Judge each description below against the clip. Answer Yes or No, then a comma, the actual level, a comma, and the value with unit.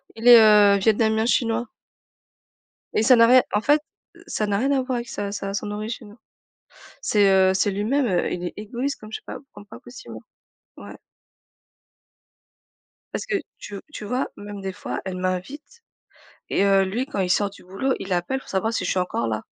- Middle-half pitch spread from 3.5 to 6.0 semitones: Yes, average, 3.8 semitones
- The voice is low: No, high, 210 Hz